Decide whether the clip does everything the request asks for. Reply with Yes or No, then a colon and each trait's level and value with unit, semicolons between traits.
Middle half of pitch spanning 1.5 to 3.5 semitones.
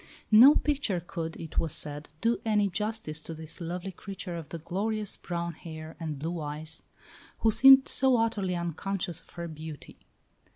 No: average, 4.8 semitones